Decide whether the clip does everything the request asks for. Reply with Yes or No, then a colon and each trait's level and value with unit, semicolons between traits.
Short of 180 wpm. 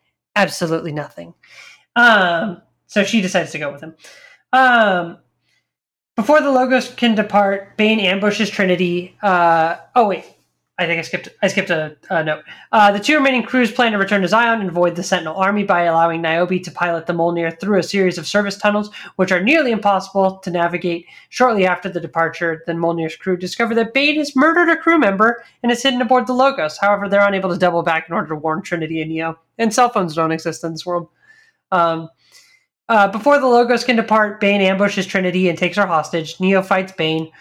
No: average, 200 wpm